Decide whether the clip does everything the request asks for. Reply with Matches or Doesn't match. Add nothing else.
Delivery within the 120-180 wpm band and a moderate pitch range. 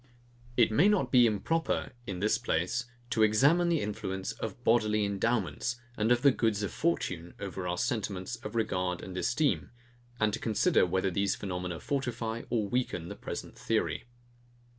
Matches